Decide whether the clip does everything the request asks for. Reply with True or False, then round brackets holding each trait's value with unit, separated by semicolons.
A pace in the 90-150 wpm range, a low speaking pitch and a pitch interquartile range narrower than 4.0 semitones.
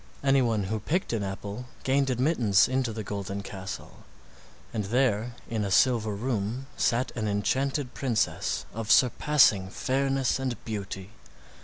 False (135 wpm; 115 Hz; 4.4 semitones)